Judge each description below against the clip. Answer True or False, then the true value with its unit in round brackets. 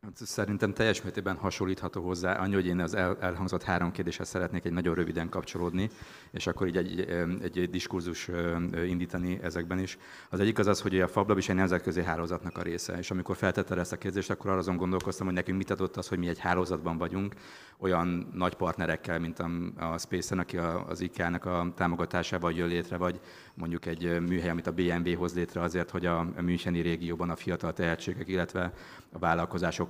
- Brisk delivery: True (190 wpm)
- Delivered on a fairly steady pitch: True (1.3 semitones)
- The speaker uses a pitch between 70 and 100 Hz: True (90 Hz)